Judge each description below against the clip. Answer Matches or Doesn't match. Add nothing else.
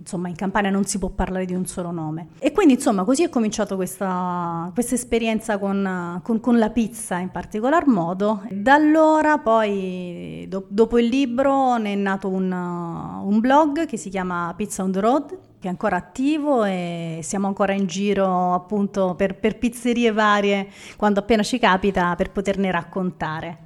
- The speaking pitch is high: Matches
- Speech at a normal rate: Doesn't match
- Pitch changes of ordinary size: Matches